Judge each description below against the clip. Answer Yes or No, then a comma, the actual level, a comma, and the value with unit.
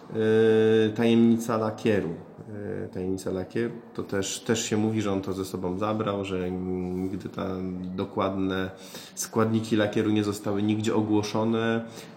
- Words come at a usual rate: Yes, average, 125 wpm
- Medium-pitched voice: No, low, 105 Hz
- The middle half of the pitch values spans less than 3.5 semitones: Yes, average, 2.8 semitones